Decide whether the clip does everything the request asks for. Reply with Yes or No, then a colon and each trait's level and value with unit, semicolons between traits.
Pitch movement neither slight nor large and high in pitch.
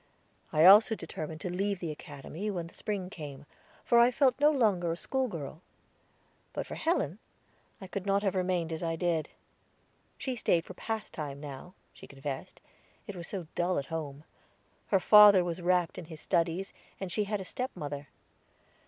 No: average, 4.1 semitones; medium, 180 Hz